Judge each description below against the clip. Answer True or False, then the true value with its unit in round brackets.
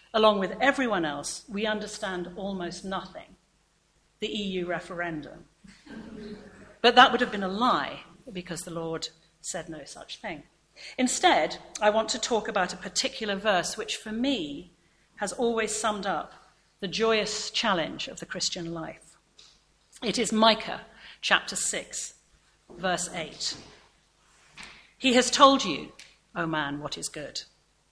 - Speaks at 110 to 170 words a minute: True (140 wpm)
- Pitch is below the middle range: False (210 Hz)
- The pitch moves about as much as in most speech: True (4.0 semitones)